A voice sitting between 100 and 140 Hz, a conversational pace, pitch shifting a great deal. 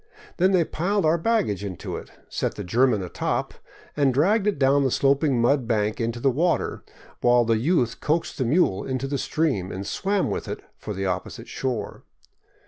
Yes: low, 135 Hz; average, 185 wpm; wide, 6.3 semitones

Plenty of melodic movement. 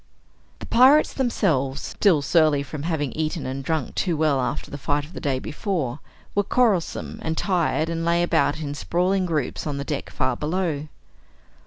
No: average, 3.6 semitones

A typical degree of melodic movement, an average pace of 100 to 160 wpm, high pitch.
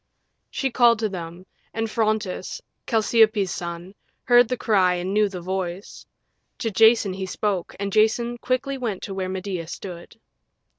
Yes: average, 3.4 semitones; average, 150 wpm; high, 200 Hz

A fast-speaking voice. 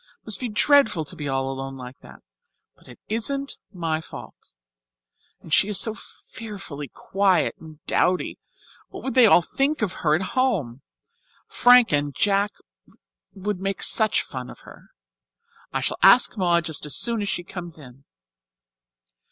No: average, 160 wpm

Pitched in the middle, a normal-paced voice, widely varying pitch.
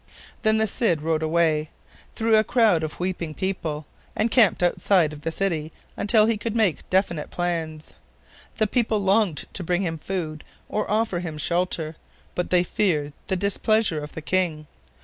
No: medium, 180 Hz; average, 170 wpm; average, 4.9 semitones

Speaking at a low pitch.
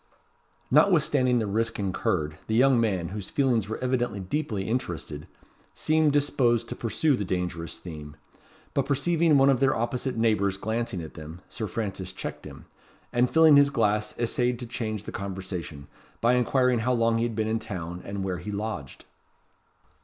Yes: low, 115 Hz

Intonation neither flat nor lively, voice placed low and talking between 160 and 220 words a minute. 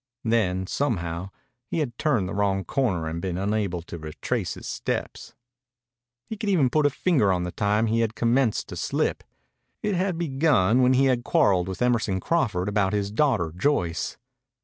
No: wide, 6.4 semitones; low, 110 Hz; average, 175 wpm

